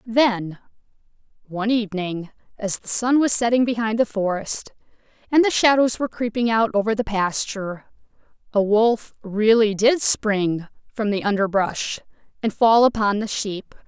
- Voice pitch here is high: Yes, high, 215 Hz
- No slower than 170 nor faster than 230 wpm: No, average, 145 wpm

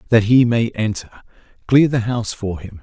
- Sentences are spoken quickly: No, average, 190 wpm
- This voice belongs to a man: Yes, male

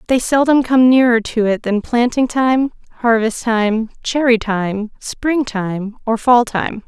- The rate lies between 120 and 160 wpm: Yes, average, 155 wpm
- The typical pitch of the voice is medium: No, high, 235 Hz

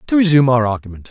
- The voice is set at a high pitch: No, low, 135 Hz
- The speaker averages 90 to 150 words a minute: No, fast, 215 wpm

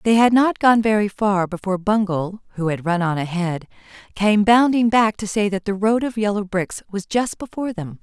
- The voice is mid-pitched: No, high, 205 Hz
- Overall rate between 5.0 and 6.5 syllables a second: Yes, 5.1 syllables/s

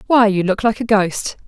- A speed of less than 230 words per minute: No, fast, 245 wpm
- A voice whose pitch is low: No, high, 210 Hz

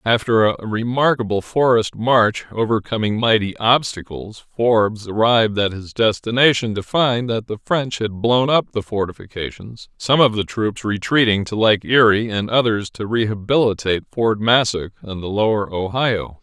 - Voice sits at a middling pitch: No, low, 110 Hz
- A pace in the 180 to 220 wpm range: No, average, 150 wpm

